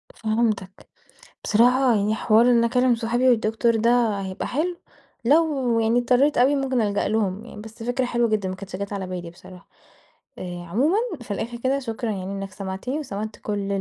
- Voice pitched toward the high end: Yes, high, 225 Hz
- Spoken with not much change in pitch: No, average, 3.6 semitones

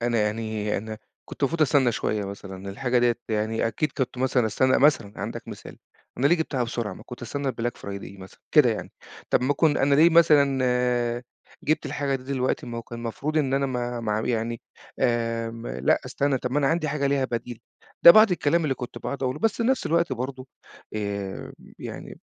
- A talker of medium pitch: No, low, 125 Hz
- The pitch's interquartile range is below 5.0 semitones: Yes, average, 4.0 semitones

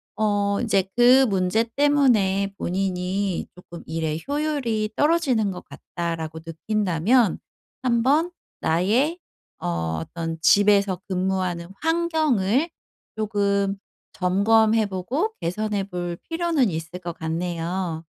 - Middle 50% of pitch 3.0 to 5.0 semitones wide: No, wide, 5.4 semitones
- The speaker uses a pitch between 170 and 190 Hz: No, high, 200 Hz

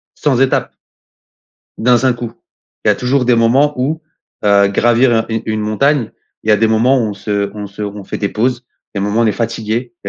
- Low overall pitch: Yes, low, 115 Hz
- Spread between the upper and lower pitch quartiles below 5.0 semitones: Yes, average, 2.9 semitones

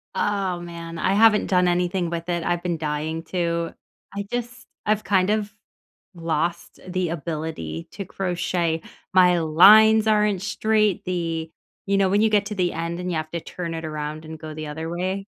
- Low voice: No, medium, 175 Hz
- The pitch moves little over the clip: No, average, 3.3 semitones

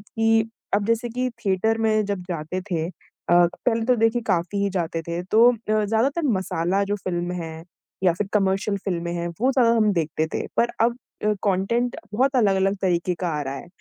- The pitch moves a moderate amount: Yes, average, 4.4 semitones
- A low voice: No, high, 195 Hz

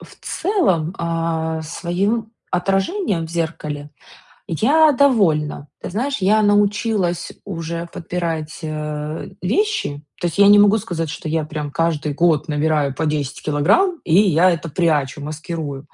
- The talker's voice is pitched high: No, medium, 165 Hz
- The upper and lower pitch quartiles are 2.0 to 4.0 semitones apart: No, average, 4.8 semitones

